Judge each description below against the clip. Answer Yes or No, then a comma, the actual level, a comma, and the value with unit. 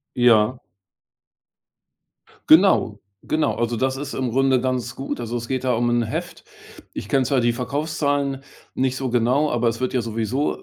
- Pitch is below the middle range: Yes, low, 130 Hz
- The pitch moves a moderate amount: No, narrow, 2.3 semitones